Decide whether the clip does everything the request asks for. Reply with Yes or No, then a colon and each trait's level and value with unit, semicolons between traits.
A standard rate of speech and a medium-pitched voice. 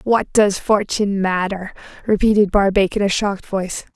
No: average, 150 wpm; high, 200 Hz